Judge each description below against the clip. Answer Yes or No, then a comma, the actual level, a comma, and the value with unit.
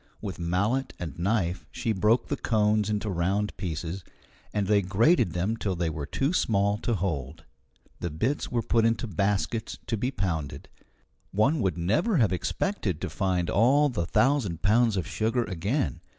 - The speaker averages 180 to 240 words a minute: No, average, 165 wpm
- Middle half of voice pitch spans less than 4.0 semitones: No, average, 4.6 semitones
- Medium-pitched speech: No, low, 100 Hz